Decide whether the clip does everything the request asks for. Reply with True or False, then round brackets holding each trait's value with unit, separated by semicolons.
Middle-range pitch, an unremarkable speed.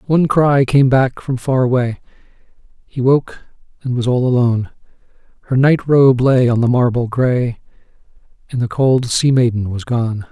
False (125 Hz; 165 wpm)